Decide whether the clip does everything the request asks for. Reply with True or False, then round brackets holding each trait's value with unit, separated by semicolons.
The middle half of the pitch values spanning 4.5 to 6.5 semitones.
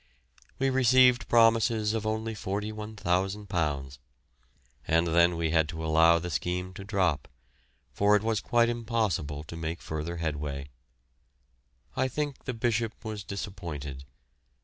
True (5.5 semitones)